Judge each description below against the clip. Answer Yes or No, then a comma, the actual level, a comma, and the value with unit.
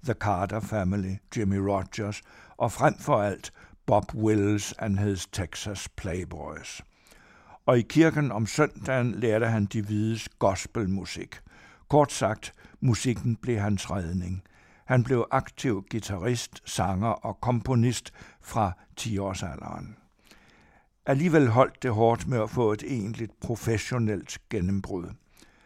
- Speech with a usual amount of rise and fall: Yes, average, 3.6 semitones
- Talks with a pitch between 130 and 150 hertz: No, low, 110 Hz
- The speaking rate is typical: No, slow, 120 wpm